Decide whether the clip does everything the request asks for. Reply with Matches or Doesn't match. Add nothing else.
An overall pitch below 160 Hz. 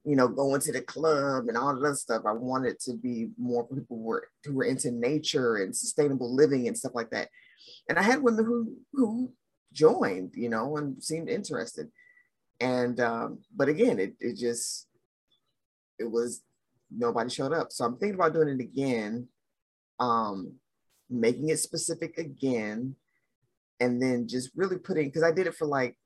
Matches